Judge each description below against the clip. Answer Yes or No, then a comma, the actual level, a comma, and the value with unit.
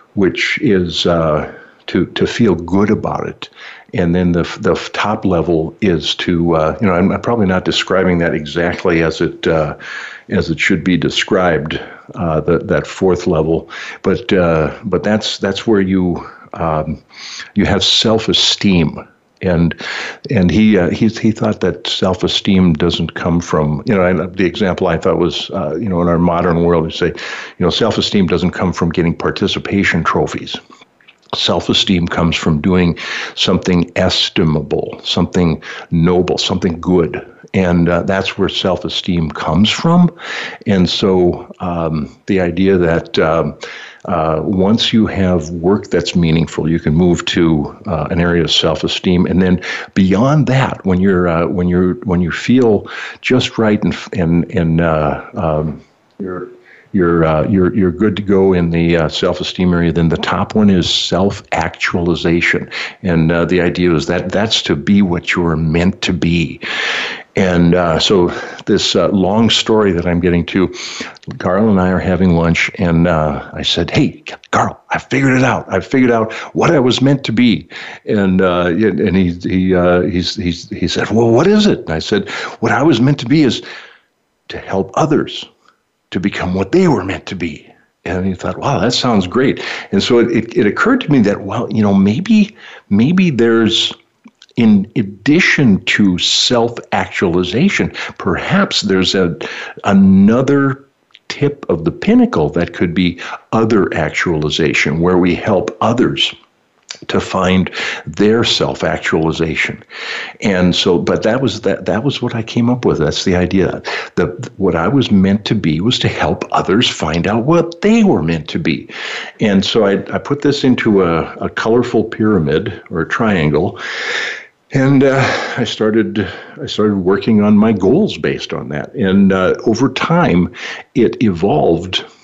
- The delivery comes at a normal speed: Yes, average, 170 wpm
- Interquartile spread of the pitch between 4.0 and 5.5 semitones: Yes, average, 4.7 semitones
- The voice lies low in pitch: Yes, very low, 90 Hz